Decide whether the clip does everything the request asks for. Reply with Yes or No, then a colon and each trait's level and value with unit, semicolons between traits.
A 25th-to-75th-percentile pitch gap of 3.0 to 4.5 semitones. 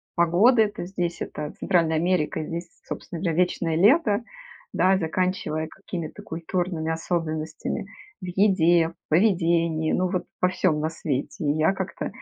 No: narrow, 2.5 semitones